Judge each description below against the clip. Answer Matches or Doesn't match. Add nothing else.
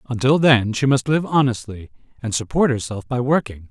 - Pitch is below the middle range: Matches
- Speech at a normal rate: Matches